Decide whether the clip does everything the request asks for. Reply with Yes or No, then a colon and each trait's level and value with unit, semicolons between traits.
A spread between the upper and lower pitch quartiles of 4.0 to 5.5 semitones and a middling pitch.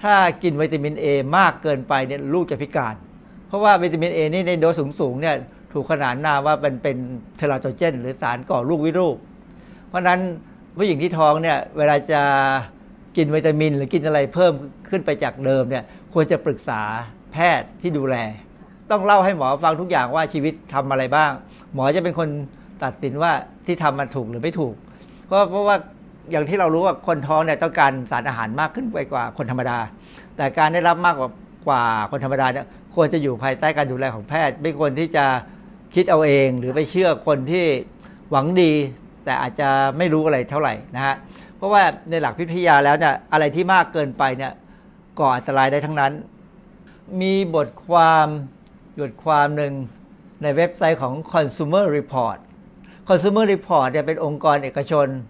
Yes: average, 4.7 semitones; medium, 155 Hz